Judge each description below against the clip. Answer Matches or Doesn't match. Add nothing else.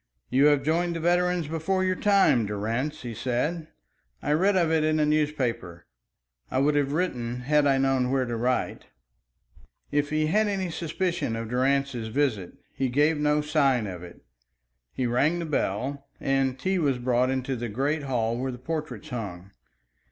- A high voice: Doesn't match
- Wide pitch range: Doesn't match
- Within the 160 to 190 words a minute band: Matches